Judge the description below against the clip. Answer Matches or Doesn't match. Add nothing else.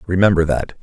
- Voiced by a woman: Doesn't match